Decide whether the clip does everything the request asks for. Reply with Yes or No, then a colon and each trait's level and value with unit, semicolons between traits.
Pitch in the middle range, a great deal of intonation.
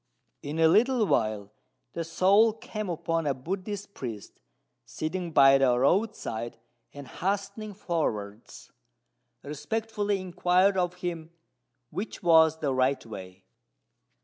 Yes: medium, 165 Hz; wide, 6.5 semitones